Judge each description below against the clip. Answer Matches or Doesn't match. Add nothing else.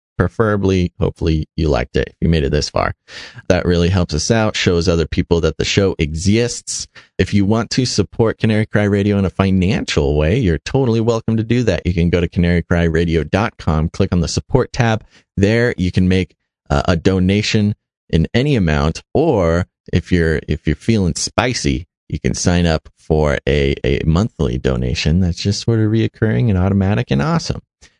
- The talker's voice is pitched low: Matches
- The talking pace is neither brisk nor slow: Matches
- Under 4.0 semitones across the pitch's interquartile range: Doesn't match